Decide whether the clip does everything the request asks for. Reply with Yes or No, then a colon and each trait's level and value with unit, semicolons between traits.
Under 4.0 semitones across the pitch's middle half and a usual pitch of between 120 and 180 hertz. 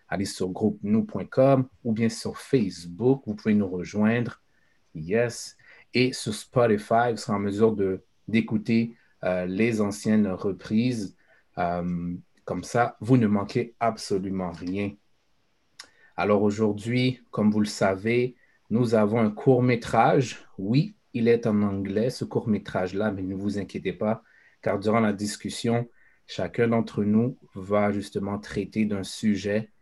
No: average, 2.7 semitones; low, 110 Hz